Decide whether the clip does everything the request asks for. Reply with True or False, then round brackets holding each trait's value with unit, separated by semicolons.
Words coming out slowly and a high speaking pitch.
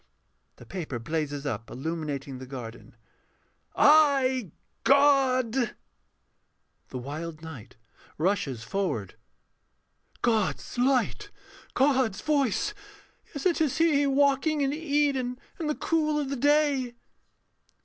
True (105 wpm; 255 Hz)